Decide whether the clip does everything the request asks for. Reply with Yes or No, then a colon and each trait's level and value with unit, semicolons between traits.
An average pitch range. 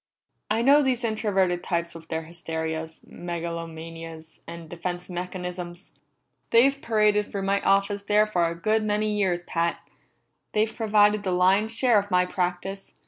Yes: average, 3.8 semitones